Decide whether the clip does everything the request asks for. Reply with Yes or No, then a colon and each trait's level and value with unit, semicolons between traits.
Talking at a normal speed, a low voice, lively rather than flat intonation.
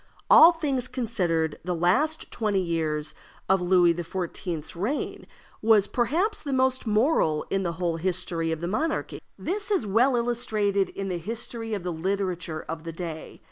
No: average, 160 wpm; high, 195 Hz; wide, 6.1 semitones